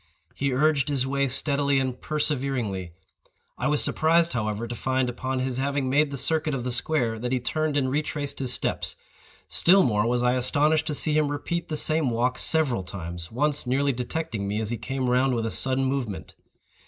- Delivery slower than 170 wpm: No, average, 190 wpm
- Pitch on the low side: Yes, low, 130 Hz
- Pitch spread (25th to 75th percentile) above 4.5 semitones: No, average, 3.3 semitones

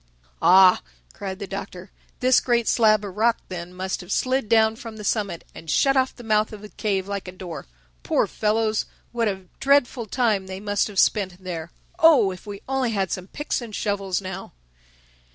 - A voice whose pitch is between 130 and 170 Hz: No, high, 205 Hz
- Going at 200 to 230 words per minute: No, average, 190 wpm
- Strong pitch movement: No, average, 3.3 semitones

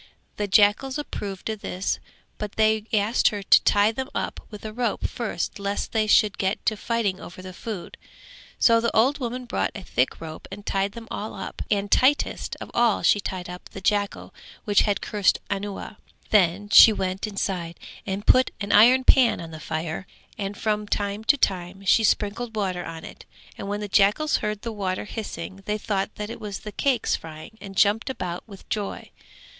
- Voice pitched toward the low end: No, high, 205 Hz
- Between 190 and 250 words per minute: Yes, average, 195 wpm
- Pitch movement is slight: Yes, narrow, 2.3 semitones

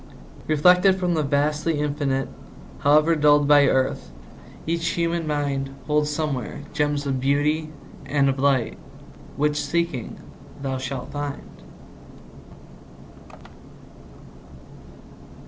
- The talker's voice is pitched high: No, medium, 145 Hz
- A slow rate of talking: Yes, slow, 95 wpm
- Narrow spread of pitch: Yes, narrow, 1.9 semitones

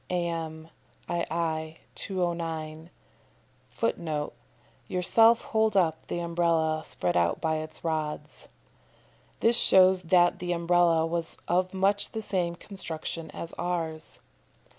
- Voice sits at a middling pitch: Yes, medium, 170 Hz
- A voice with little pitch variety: Yes, narrow, 2.2 semitones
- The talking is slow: Yes, slow, 115 wpm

